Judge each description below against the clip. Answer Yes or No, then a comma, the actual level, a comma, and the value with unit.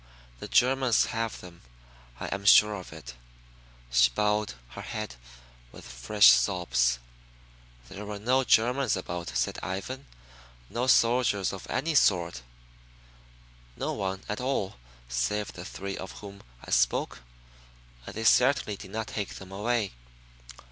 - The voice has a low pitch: Yes, low, 100 Hz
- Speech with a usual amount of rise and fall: Yes, average, 4.3 semitones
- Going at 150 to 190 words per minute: No, slow, 135 wpm